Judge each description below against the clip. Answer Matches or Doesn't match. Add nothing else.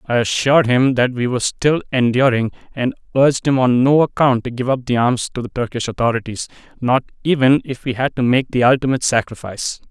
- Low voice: Matches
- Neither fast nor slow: Matches